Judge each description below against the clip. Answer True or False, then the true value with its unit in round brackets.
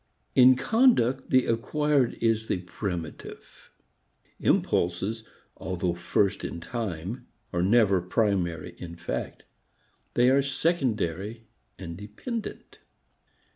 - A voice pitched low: True (110 Hz)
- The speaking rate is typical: False (95 wpm)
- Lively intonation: True (6.2 semitones)